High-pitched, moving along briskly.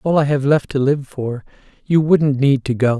No: medium, 140 Hz; fast, 240 wpm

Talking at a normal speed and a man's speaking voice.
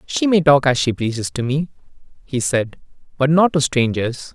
Yes: average, 195 wpm; male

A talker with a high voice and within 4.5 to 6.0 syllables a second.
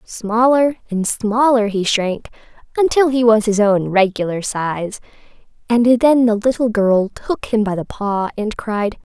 No: high, 220 Hz; 4.0 syllables/s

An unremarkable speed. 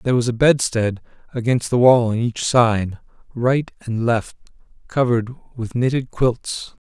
Yes: average, 150 wpm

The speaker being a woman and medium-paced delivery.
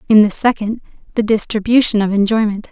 Yes: female; average, 155 wpm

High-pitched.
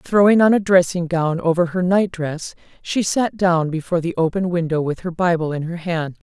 No: medium, 175 Hz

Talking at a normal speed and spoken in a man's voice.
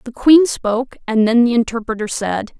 No: average, 185 wpm; female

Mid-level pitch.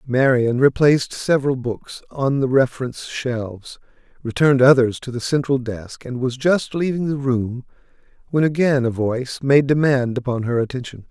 No: low, 130 Hz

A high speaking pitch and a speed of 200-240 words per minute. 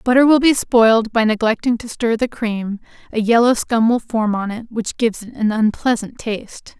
Yes: high, 225 Hz; fast, 205 wpm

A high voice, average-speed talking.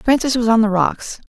No: high, 230 Hz; fast, 230 wpm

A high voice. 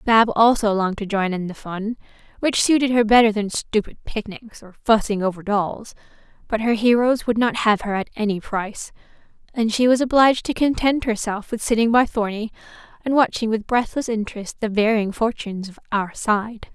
Yes: high, 220 Hz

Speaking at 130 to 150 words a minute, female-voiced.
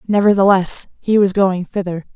Yes: average, 140 wpm; female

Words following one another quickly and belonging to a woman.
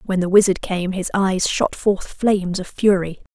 No: average, 195 wpm; female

